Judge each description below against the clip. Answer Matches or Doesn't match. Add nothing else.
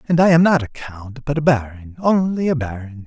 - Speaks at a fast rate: Matches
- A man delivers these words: Matches